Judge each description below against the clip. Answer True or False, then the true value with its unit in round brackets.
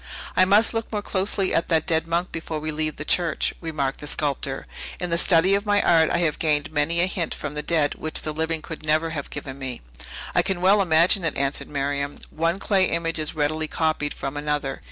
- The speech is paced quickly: True (220 wpm)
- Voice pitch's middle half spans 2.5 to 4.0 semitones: True (2.8 semitones)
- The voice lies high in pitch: False (160 Hz)